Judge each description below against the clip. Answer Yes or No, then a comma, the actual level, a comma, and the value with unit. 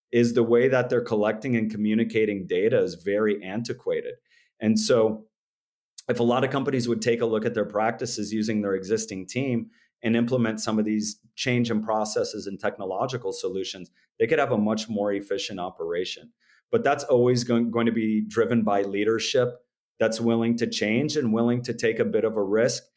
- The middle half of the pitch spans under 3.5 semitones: Yes, narrow, 2.4 semitones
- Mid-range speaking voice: No, low, 115 Hz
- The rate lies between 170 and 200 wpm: Yes, average, 185 wpm